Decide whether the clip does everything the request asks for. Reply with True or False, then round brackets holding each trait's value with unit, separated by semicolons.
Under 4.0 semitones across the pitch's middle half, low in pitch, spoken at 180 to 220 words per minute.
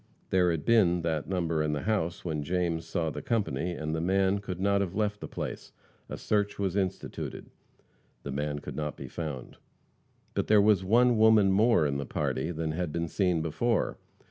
False (4.3 semitones; 90 Hz; 195 wpm)